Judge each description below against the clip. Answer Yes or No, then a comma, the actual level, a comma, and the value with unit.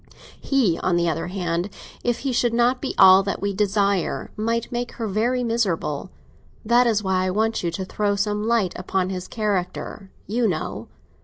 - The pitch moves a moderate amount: Yes, average, 3.9 semitones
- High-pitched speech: Yes, high, 205 Hz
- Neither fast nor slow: Yes, average, 180 wpm